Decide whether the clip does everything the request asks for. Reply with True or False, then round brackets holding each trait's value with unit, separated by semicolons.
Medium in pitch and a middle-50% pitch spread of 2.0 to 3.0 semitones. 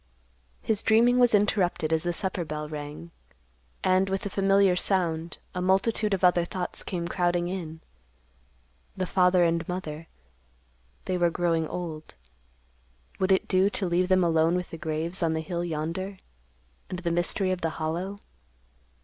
True (175 Hz; 2.7 semitones)